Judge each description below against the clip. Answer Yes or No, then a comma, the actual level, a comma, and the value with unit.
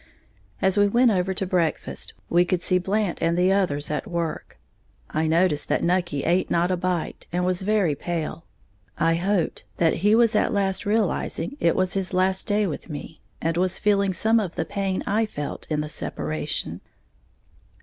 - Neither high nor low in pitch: Yes, medium, 180 Hz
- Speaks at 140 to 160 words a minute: No, average, 180 wpm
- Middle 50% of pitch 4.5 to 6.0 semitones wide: No, average, 3.1 semitones